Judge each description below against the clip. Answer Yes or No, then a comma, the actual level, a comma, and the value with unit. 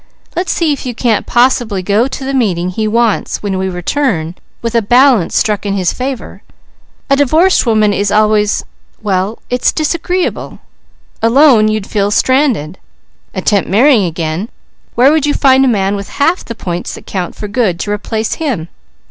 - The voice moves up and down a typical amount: Yes, average, 4.9 semitones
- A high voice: Yes, high, 220 Hz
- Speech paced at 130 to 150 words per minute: No, average, 170 wpm